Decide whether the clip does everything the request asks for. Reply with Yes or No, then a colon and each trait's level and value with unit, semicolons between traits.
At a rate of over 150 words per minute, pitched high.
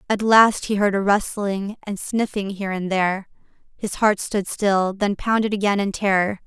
Yes: average, 185 wpm; high, 200 Hz